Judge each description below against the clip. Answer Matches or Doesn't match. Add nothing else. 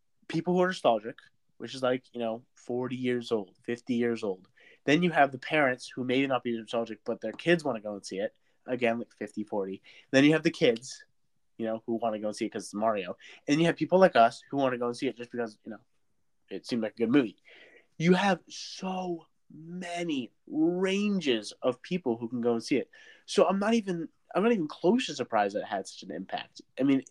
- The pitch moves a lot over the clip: Matches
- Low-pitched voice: Matches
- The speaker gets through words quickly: Matches